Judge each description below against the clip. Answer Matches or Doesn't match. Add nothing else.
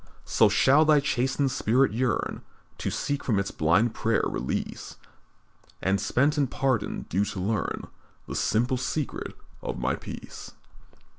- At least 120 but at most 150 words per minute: Matches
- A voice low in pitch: Matches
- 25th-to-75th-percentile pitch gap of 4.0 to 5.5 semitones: Matches